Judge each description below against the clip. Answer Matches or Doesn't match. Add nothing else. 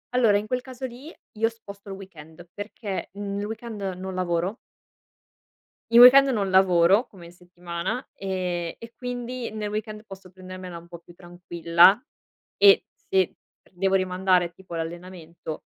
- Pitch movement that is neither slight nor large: Matches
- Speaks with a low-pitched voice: Doesn't match